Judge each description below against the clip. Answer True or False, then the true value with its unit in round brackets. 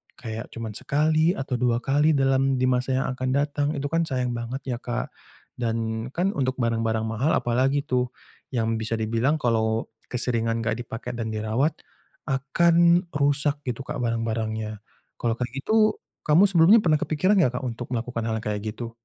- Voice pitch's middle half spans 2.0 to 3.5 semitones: False (4.0 semitones)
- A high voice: False (125 Hz)